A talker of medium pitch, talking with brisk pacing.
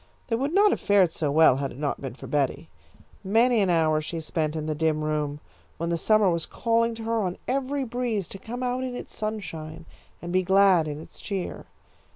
Yes: medium, 180 Hz; fast, 215 wpm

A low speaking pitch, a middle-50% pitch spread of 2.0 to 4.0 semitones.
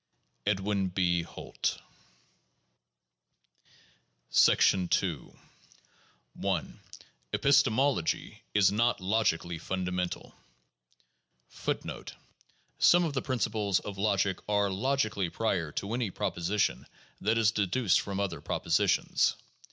Yes: low, 100 Hz; average, 3.3 semitones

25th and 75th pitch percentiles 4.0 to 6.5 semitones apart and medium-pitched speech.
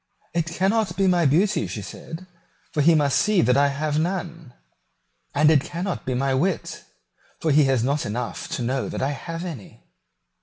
Yes: average, 4.3 semitones; medium, 155 Hz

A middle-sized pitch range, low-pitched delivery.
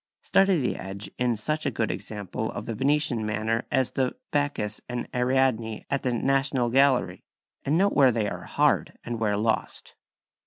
Yes: average, 3.9 semitones; low, 125 Hz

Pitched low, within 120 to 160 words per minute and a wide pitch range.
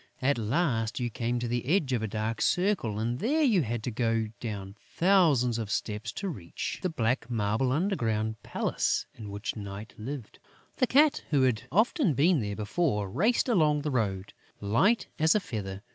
No: low, 120 Hz; average, 180 wpm; wide, 7.4 semitones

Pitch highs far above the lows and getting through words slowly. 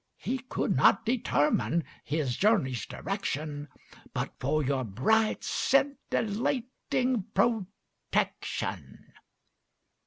Yes: wide, 8.5 semitones; slow, 75 wpm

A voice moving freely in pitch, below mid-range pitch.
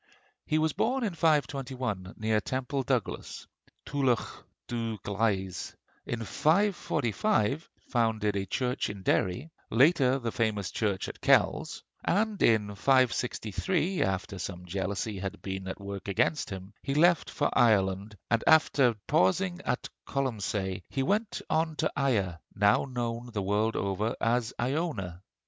Yes: wide, 5.8 semitones; low, 115 Hz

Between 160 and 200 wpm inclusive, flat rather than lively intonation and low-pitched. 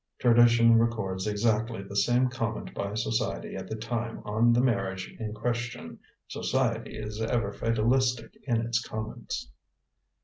No: slow, 135 wpm; narrow, 1.9 semitones; low, 115 Hz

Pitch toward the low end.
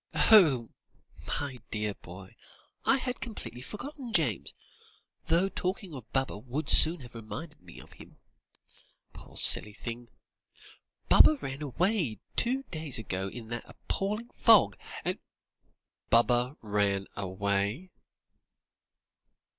Yes: low, 130 Hz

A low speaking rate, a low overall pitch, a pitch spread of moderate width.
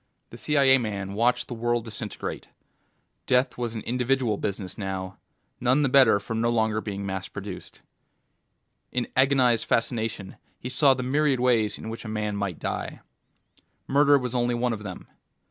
No: average, 165 wpm; low, 115 Hz; average, 3.4 semitones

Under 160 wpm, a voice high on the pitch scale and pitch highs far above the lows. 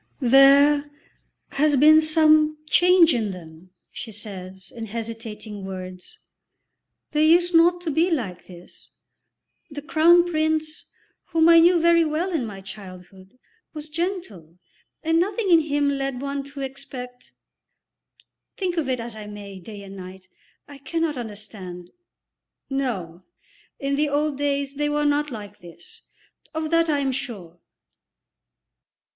Yes: average, 140 wpm; very high, 275 Hz; wide, 7.2 semitones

